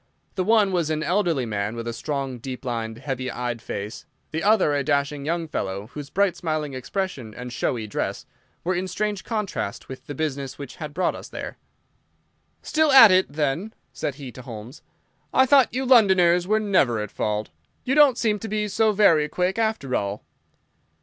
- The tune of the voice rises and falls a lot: Yes, wide, 8.0 semitones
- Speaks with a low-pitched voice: No, medium, 155 Hz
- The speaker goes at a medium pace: Yes, average, 185 wpm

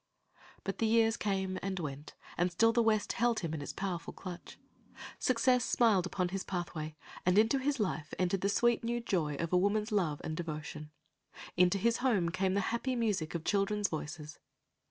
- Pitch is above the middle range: Yes, high, 195 Hz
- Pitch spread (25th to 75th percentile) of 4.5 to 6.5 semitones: Yes, average, 4.8 semitones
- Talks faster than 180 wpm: Yes, average, 190 wpm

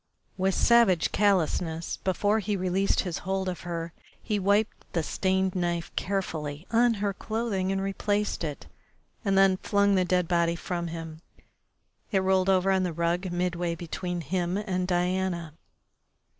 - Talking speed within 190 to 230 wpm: No, average, 150 wpm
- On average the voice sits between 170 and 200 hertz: Yes, medium, 185 Hz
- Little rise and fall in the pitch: Yes, narrow, 2.2 semitones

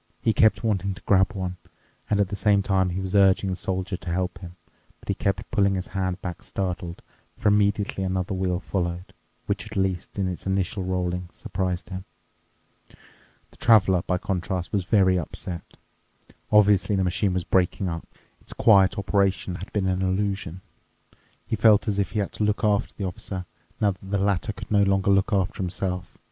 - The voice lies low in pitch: Yes, very low, 95 Hz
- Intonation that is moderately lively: No, narrow, 1.7 semitones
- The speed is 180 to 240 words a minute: Yes, average, 185 wpm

